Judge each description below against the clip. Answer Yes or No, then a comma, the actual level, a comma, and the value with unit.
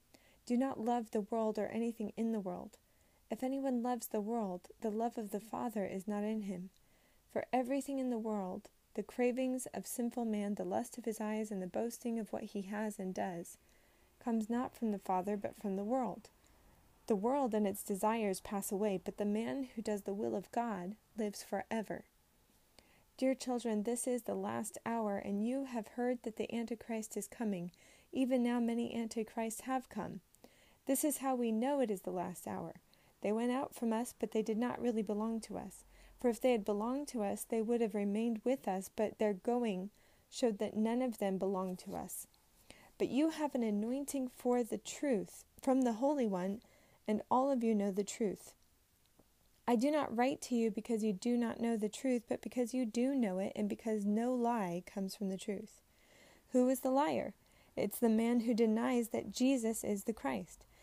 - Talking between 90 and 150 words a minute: No, average, 200 wpm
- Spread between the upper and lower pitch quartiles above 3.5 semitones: No, average, 2.9 semitones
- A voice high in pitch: Yes, high, 225 Hz